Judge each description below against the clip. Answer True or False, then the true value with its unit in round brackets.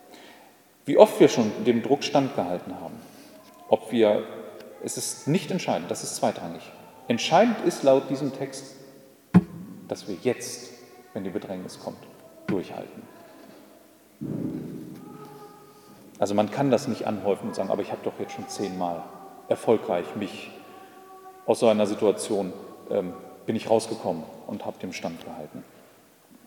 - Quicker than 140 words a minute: False (135 wpm)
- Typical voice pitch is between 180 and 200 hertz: False (135 Hz)